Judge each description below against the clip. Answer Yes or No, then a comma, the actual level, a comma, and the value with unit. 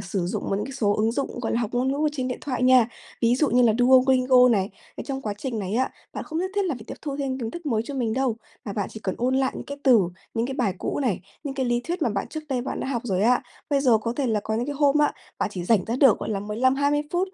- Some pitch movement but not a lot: Yes, average, 3.6 semitones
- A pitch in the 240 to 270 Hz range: Yes, very high, 250 Hz